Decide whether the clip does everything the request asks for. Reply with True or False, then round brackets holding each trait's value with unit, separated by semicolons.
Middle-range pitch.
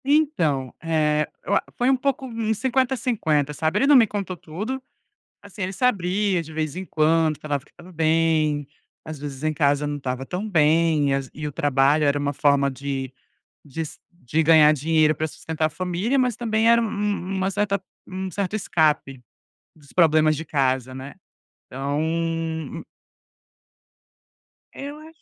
True (160 Hz)